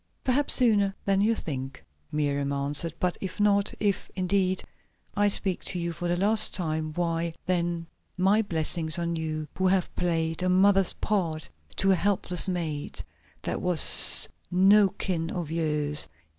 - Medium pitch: Yes, medium, 175 Hz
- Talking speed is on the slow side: No, average, 155 wpm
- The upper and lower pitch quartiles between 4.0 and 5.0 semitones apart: No, average, 3.4 semitones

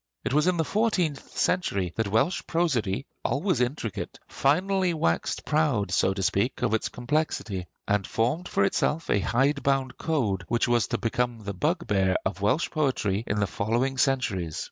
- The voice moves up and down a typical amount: No, wide, 7.1 semitones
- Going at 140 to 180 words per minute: Yes, average, 165 wpm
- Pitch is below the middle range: Yes, low, 125 Hz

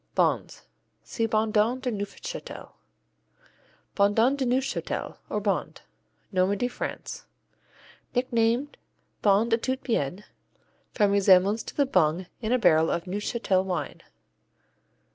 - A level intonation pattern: No, average, 4.1 semitones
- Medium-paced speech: No, slow, 110 wpm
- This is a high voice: Yes, high, 215 Hz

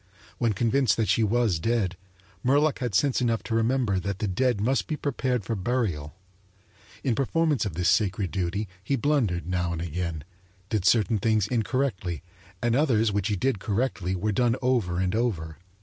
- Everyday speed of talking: Yes, average, 175 wpm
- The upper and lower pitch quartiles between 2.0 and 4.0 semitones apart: No, average, 5.1 semitones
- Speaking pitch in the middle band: No, low, 110 Hz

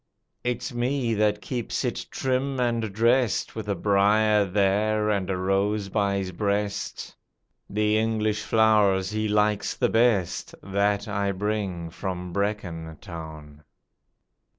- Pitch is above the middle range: No, low, 105 Hz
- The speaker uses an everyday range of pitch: No, narrow, 1.9 semitones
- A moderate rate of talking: No, slow, 130 wpm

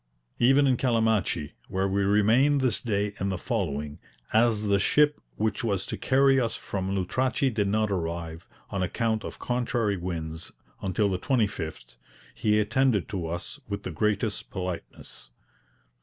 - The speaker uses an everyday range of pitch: Yes, average, 4.3 semitones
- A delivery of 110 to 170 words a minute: Yes, average, 155 wpm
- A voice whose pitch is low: Yes, low, 105 Hz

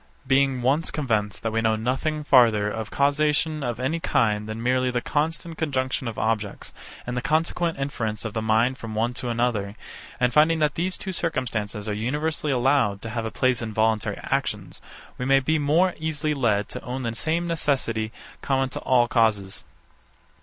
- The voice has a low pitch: Yes, low, 125 Hz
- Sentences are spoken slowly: No, average, 180 wpm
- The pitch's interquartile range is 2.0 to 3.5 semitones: No, average, 4.9 semitones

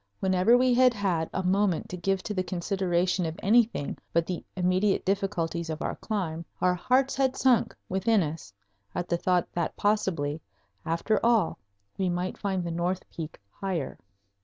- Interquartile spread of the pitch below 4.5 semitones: Yes, average, 3.3 semitones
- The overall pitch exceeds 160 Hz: Yes, medium, 185 Hz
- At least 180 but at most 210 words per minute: No, average, 165 wpm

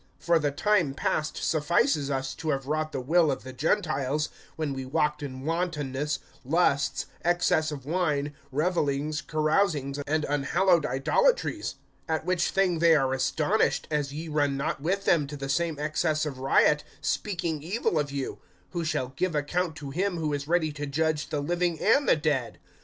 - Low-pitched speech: No, medium, 155 Hz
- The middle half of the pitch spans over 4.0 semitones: No, average, 3.3 semitones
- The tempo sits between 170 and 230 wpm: Yes, average, 175 wpm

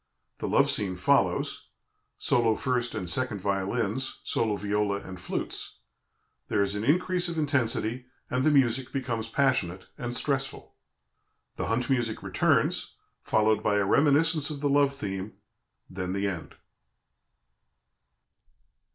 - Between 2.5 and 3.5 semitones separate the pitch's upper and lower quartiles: No, average, 5.3 semitones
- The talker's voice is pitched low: Yes, low, 115 Hz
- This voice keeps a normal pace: No, slow, 130 wpm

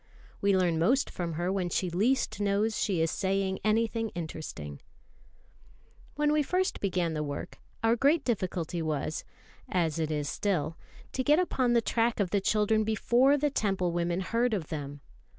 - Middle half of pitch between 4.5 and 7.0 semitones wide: Yes, wide, 5.4 semitones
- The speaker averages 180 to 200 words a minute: No, average, 170 wpm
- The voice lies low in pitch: No, high, 195 Hz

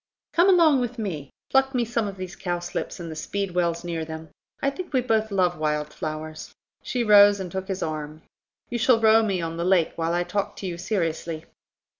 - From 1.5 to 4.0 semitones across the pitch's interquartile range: No, average, 5.3 semitones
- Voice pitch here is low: No, medium, 185 Hz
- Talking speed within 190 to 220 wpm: Yes, fast, 205 wpm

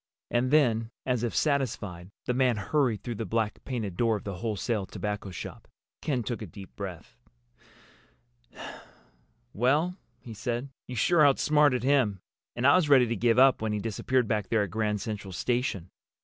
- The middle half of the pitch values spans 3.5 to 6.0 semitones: Yes, average, 3.8 semitones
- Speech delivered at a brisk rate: No, average, 170 wpm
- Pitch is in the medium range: No, low, 115 Hz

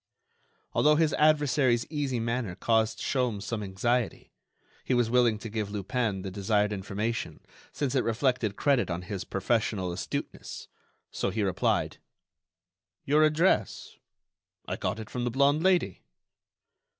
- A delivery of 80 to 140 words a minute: Yes, slow, 135 wpm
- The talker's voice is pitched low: Yes, low, 115 Hz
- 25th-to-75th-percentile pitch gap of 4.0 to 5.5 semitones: Yes, average, 4.4 semitones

